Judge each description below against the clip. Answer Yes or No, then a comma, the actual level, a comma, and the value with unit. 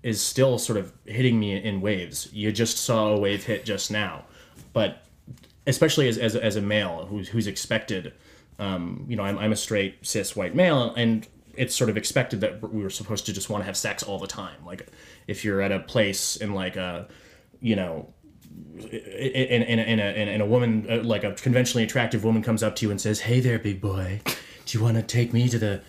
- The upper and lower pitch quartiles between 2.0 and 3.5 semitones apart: Yes, narrow, 2.5 semitones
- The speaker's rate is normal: No, fast, 225 wpm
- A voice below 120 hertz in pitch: Yes, low, 110 Hz